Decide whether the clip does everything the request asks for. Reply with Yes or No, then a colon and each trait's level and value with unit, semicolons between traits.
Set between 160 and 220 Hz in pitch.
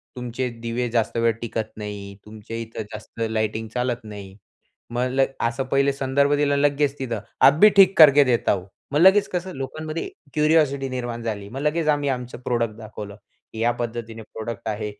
No: low, 120 Hz